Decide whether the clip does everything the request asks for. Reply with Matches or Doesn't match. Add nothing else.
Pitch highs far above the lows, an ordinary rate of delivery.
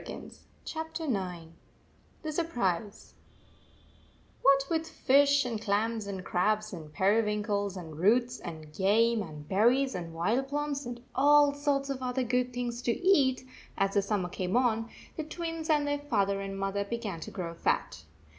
Matches